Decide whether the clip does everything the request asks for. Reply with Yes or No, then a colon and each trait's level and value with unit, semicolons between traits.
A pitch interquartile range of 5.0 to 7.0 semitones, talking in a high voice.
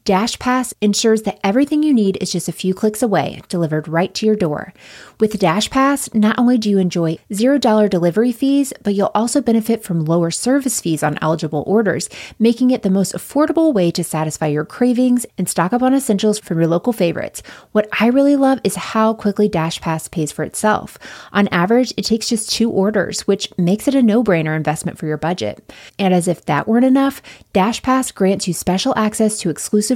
Yes: average, 5.3 semitones; high, 210 Hz